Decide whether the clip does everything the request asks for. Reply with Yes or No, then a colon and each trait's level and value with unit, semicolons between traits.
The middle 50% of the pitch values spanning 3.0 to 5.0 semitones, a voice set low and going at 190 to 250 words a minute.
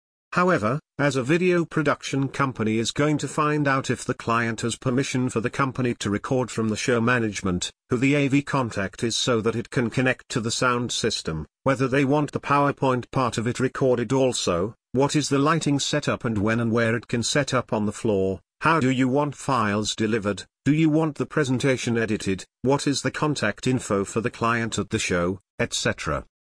Yes: average, 3.9 semitones; low, 125 Hz; average, 200 wpm